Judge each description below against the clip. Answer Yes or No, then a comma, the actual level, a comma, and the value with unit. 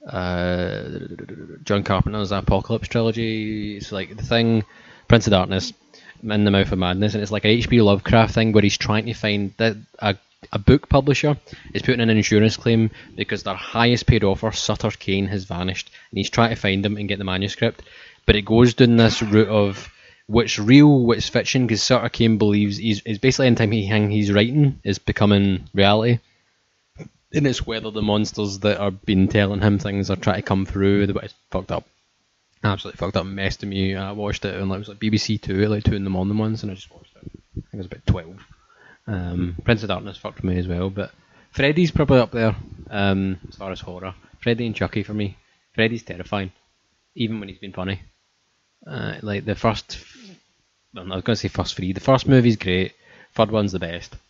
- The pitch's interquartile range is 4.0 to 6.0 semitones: No, narrow, 2.6 semitones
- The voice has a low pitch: Yes, low, 105 Hz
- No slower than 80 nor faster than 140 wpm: No, fast, 205 wpm